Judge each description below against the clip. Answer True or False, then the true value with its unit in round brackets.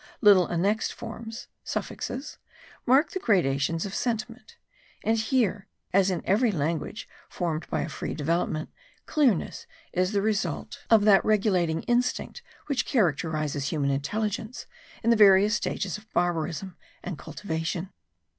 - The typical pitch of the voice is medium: False (195 Hz)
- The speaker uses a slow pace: True (130 wpm)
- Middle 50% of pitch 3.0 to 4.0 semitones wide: False (5.0 semitones)